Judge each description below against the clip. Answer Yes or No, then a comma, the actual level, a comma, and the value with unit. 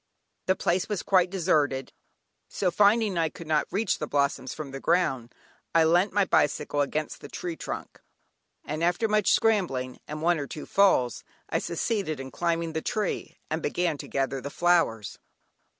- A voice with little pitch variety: No, average, 4.5 semitones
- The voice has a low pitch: No, medium, 165 Hz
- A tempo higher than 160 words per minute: Yes, average, 170 wpm